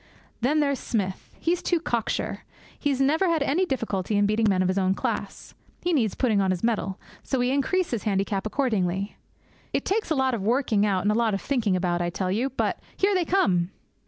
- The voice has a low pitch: No, high, 225 Hz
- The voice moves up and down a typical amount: No, wide, 6.3 semitones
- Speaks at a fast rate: Yes, fast, 215 wpm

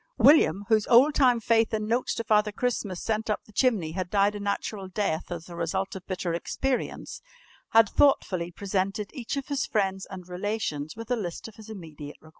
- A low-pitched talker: No, high, 205 Hz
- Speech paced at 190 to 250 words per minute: Yes, average, 200 wpm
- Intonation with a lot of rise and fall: No, average, 3.8 semitones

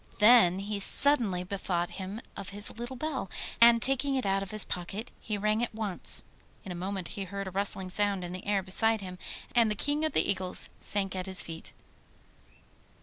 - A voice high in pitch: Yes, high, 200 Hz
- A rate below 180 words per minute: No, average, 200 wpm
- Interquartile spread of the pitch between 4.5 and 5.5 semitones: No, average, 3.1 semitones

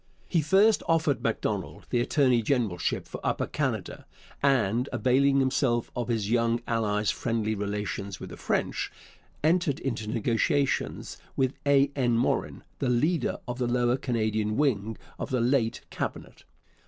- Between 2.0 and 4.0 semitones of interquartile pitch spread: Yes, average, 3.6 semitones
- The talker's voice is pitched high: No, low, 120 Hz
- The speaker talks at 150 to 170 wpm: No, average, 140 wpm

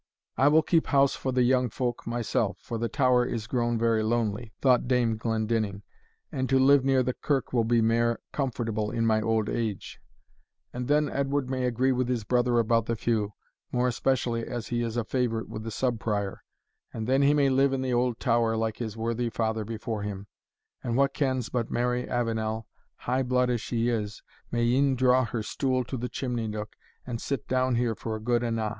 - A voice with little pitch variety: Yes, narrow, 2.3 semitones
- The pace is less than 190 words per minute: No, fast, 205 wpm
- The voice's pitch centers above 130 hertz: No, low, 120 Hz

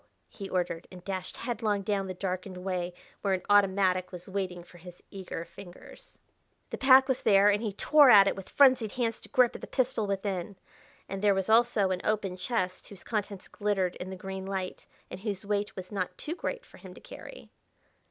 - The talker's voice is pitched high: Yes, high, 195 Hz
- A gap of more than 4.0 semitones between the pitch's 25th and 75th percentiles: No, average, 2.7 semitones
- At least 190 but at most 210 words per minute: Yes, average, 200 wpm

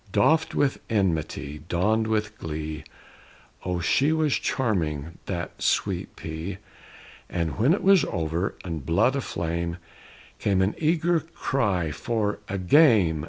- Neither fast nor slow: No, slow, 125 wpm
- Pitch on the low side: Yes, very low, 95 Hz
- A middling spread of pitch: No, wide, 7.8 semitones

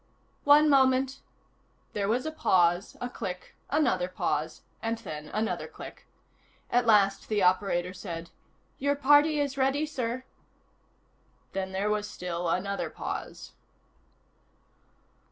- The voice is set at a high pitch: Yes, high, 215 Hz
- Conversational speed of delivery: No, slow, 120 wpm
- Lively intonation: Yes, wide, 6.6 semitones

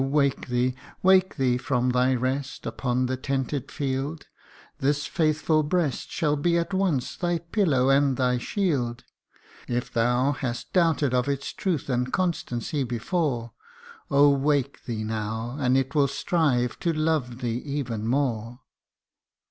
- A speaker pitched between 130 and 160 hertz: Yes, low, 135 Hz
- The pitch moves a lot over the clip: No, average, 3.6 semitones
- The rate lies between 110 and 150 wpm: Yes, average, 140 wpm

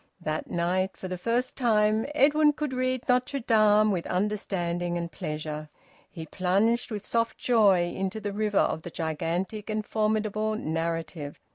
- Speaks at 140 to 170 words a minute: Yes, average, 150 wpm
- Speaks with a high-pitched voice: Yes, high, 205 Hz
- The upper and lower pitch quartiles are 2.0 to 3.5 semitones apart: No, average, 4.4 semitones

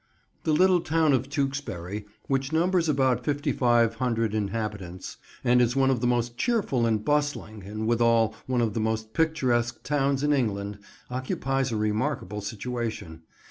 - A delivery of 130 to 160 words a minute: Yes, average, 145 wpm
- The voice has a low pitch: Yes, low, 120 Hz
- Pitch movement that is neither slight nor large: Yes, average, 4.1 semitones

